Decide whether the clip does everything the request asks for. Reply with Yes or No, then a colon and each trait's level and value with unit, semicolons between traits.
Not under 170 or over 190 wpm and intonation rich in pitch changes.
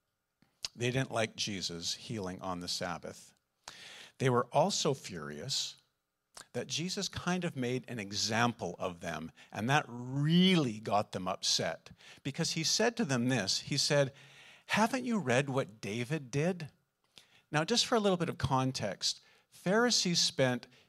No: average, 145 wpm; wide, 7.6 semitones